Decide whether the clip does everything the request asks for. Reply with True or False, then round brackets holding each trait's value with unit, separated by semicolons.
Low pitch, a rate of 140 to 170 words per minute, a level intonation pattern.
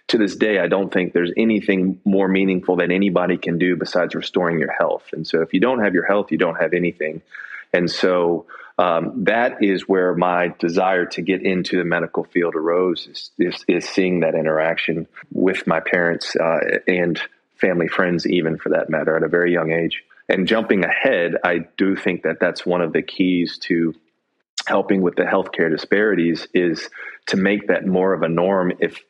False (90 Hz; 195 wpm; 1.7 semitones)